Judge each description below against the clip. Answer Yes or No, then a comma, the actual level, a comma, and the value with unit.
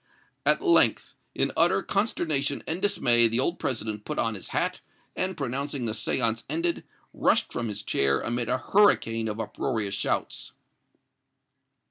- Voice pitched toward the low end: Yes, low, 120 Hz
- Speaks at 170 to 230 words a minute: No, average, 145 wpm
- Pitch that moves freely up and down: Yes, wide, 6.0 semitones